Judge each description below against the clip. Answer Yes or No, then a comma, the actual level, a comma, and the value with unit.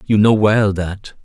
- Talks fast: No, average, 195 wpm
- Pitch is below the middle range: Yes, low, 105 Hz